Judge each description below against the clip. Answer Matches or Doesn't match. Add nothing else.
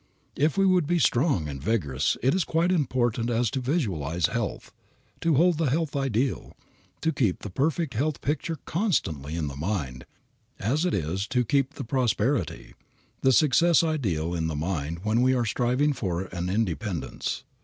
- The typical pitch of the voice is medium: Doesn't match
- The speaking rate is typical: Matches